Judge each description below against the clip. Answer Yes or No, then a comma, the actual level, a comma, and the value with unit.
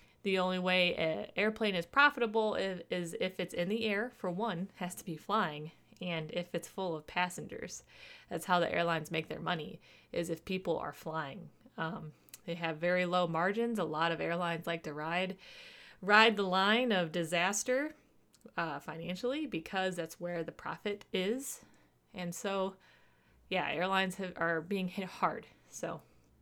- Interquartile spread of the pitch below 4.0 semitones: Yes, average, 3.5 semitones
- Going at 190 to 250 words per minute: No, average, 165 wpm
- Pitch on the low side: No, medium, 180 Hz